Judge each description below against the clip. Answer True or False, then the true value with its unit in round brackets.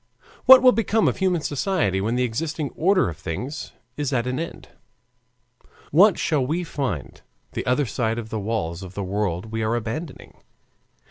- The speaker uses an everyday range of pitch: False (7.1 semitones)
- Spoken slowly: False (175 wpm)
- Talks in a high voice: False (125 Hz)